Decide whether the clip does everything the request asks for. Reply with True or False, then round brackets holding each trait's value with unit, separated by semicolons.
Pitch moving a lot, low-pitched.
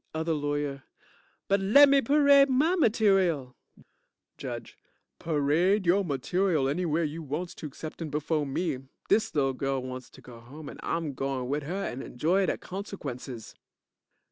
False (6.0 semitones; 155 Hz)